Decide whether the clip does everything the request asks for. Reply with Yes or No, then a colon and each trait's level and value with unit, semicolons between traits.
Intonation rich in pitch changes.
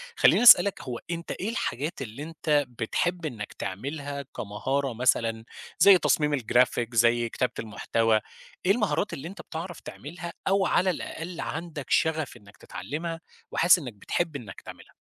Yes: wide, 6.3 semitones